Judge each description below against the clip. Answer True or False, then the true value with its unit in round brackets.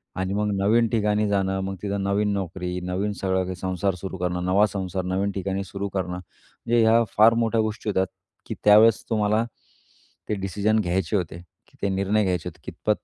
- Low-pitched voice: True (100 Hz)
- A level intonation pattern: True (2.2 semitones)